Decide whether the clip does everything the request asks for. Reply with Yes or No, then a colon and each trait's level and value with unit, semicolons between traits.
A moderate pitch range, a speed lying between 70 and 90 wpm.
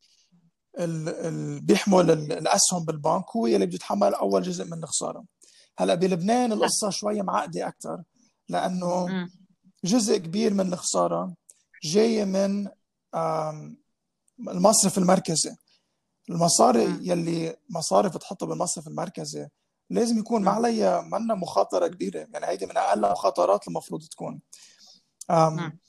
No: average, 4.1 semitones; average, 105 wpm